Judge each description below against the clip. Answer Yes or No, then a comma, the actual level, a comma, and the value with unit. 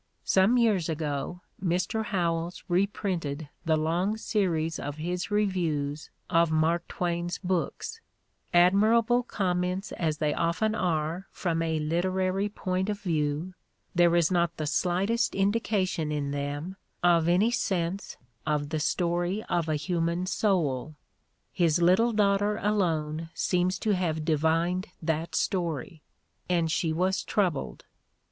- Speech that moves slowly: Yes, slow, 125 wpm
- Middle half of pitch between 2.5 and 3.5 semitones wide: Yes, average, 3.1 semitones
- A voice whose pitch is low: No, medium, 175 Hz